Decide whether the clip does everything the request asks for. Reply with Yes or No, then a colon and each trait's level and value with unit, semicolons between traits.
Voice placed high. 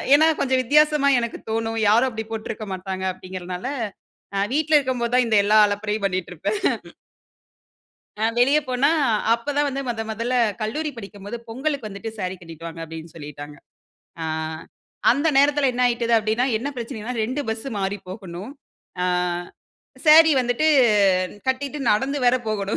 Yes: high, 230 Hz